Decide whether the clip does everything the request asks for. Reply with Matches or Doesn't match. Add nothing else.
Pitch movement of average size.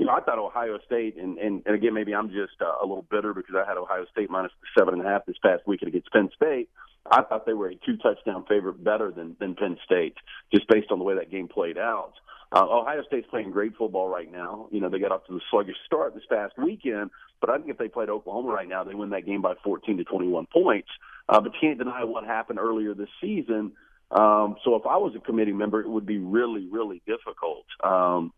Matches